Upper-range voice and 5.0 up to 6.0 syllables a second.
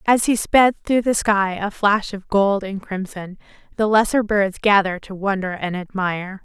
No: high, 200 Hz; 4.7 syllables/s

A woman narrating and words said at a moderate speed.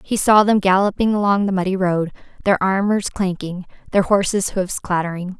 Yes: female; average, 165 wpm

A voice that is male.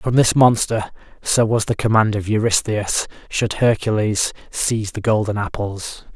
Yes: male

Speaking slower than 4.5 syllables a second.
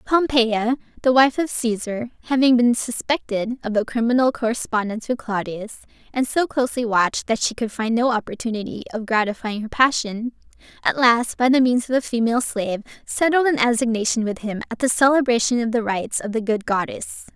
No: 5.6 syllables/s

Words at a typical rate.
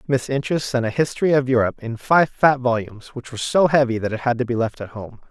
No: fast, 260 wpm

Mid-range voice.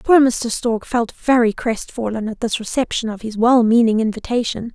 No: high, 230 Hz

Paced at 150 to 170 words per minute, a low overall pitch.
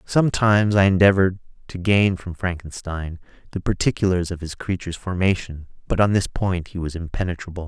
Yes: average, 155 wpm; very low, 90 Hz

